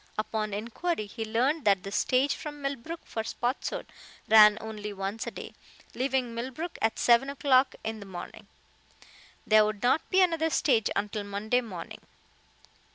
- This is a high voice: Yes, high, 230 Hz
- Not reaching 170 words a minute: Yes, average, 155 wpm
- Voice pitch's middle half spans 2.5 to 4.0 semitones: No, average, 4.4 semitones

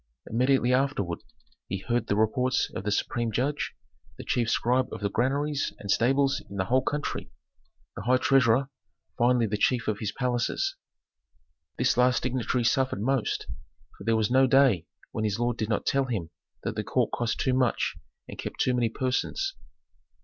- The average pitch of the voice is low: Yes, low, 125 Hz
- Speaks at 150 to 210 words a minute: Yes, average, 175 wpm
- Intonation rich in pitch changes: No, average, 3.1 semitones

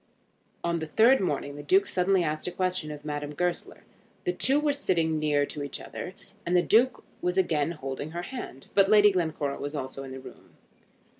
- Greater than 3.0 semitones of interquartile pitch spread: Yes, average, 4.5 semitones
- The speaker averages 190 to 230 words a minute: Yes, fast, 205 wpm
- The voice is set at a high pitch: No, medium, 170 Hz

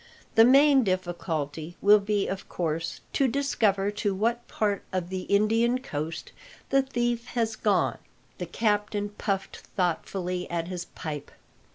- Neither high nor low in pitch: No, high, 200 Hz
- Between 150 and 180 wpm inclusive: No, average, 140 wpm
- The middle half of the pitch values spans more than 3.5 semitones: Yes, average, 4.3 semitones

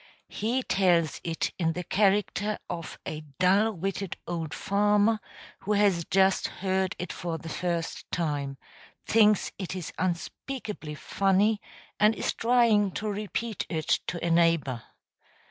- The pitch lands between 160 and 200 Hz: Yes, high, 190 Hz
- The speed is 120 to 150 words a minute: Yes, slow, 135 wpm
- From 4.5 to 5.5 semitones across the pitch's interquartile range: No, average, 3.7 semitones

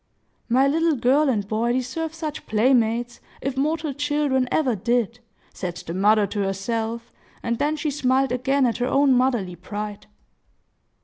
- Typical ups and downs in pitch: Yes, average, 4.1 semitones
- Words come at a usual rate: Yes, average, 150 wpm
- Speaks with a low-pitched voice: No, very high, 250 Hz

